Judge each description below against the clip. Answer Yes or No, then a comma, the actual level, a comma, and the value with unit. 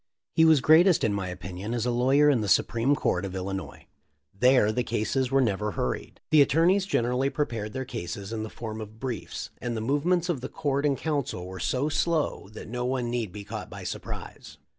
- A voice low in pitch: Yes, low, 120 Hz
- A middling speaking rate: No, fast, 210 wpm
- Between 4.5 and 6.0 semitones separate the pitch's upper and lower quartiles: Yes, average, 5.0 semitones